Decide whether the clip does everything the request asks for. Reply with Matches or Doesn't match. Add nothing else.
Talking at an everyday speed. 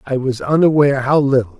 Matches